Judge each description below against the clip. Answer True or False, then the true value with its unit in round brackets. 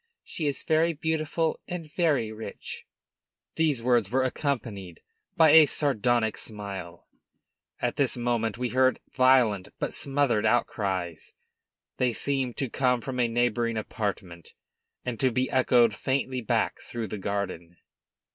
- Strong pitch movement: False (4.2 semitones)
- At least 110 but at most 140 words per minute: True (135 wpm)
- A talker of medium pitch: False (120 Hz)